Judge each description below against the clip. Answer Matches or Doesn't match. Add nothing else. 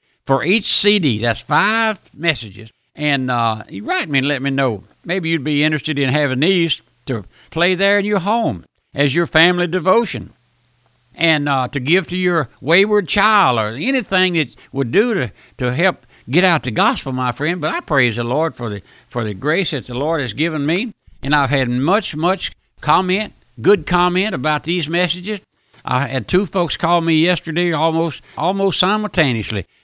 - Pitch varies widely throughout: Matches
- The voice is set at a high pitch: Doesn't match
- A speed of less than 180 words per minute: Doesn't match